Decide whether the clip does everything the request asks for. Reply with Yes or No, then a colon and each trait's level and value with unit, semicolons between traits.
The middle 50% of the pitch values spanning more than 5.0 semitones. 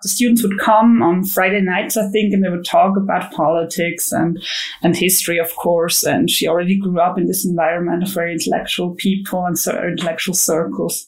No: narrow, 2.6 semitones